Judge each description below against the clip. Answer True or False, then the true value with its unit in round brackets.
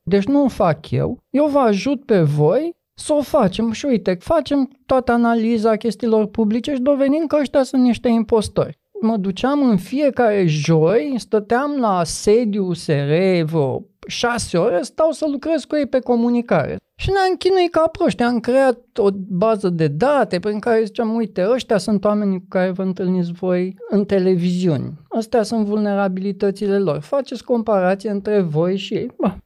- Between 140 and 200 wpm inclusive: True (165 wpm)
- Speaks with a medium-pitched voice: False (225 Hz)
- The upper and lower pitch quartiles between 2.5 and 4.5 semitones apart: False (5.1 semitones)